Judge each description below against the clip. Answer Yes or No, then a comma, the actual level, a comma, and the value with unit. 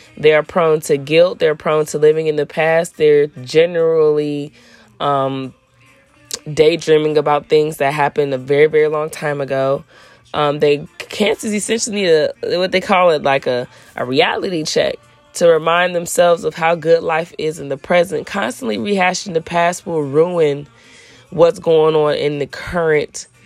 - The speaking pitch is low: No, medium, 155 Hz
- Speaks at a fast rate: No, average, 165 wpm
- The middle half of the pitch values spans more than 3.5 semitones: No, average, 2.8 semitones